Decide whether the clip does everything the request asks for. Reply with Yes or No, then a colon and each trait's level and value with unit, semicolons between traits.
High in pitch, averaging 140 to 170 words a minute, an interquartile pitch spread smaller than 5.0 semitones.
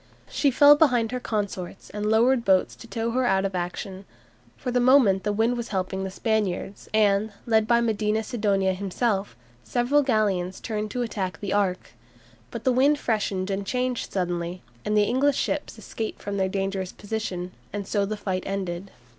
No: high, 210 Hz; average, 180 wpm; average, 3.6 semitones